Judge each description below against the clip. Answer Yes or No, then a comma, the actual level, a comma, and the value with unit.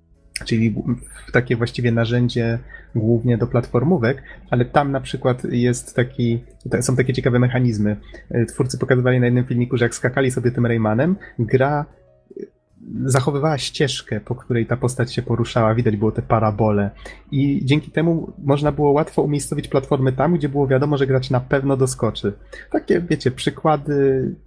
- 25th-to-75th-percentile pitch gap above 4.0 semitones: No, average, 2.9 semitones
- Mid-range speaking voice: No, low, 125 Hz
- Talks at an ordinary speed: Yes, average, 150 wpm